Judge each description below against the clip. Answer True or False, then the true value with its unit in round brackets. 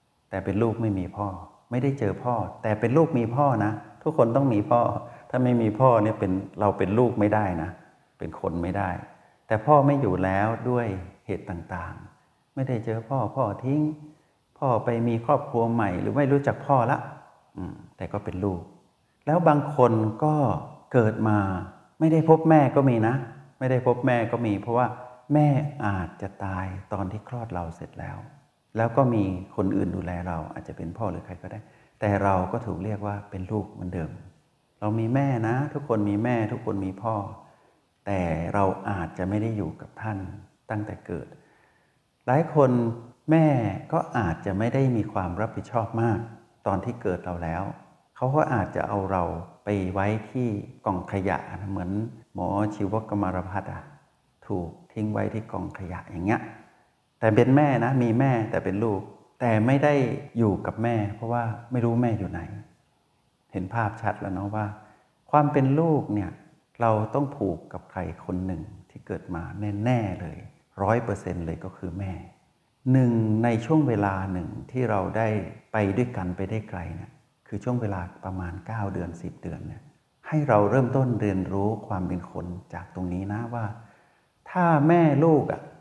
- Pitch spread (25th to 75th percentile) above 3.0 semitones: True (4.1 semitones)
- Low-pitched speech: True (110 Hz)